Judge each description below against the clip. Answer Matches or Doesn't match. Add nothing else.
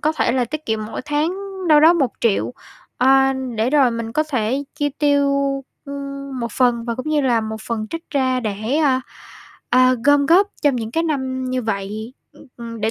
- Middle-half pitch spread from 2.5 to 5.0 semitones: Matches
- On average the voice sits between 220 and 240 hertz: Doesn't match